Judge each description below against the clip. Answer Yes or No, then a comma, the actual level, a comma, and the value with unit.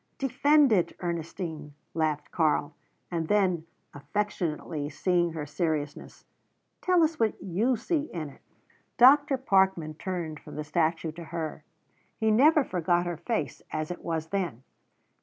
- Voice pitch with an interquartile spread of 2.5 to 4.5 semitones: No, average, 5.3 semitones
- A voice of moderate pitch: Yes, medium, 175 Hz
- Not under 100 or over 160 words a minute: Yes, average, 140 wpm